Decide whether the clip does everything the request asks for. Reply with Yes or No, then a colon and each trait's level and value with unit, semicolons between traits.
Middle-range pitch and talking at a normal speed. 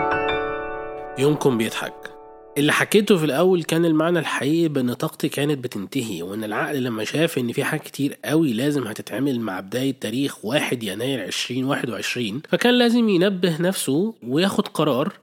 No: medium, 150 Hz; fast, 140 wpm